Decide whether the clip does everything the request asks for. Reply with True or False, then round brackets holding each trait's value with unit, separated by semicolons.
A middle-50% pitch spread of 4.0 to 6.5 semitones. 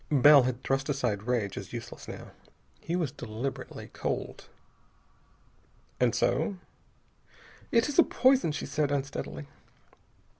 True (4.3 semitones)